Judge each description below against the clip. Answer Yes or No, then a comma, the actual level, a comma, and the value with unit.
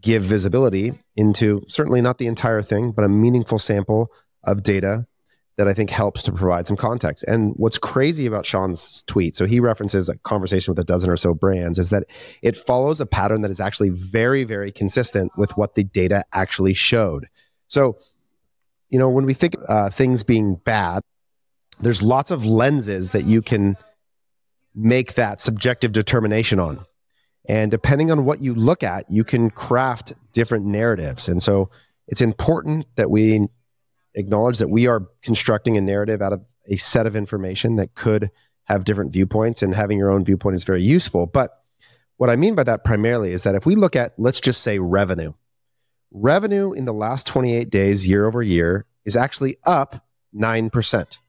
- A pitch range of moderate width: Yes, average, 3.5 semitones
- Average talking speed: Yes, average, 180 wpm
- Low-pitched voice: Yes, low, 110 Hz